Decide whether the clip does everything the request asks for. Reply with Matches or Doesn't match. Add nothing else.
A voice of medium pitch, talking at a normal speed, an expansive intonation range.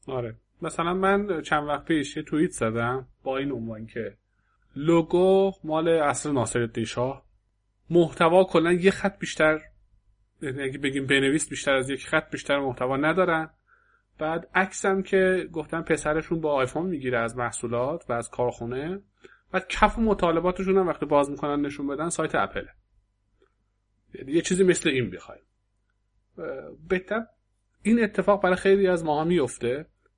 Matches